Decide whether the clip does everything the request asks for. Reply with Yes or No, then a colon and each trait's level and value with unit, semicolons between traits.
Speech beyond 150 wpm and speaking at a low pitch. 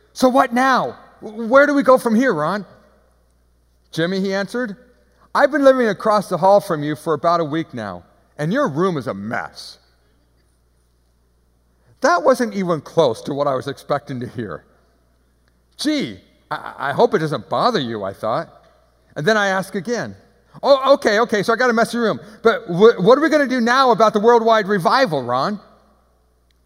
No: average, 180 wpm; high, 190 Hz